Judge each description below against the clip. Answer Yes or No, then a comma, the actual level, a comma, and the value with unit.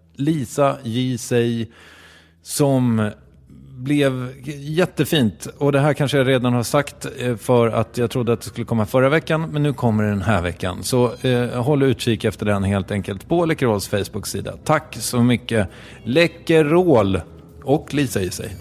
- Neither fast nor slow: Yes, average, 160 wpm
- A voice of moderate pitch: No, low, 120 Hz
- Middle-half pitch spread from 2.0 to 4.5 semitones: No, wide, 5.6 semitones